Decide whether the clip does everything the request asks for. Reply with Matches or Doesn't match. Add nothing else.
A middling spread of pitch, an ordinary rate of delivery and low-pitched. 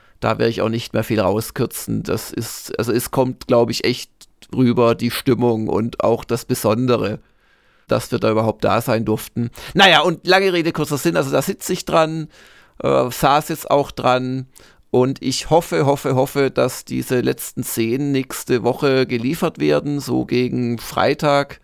Matches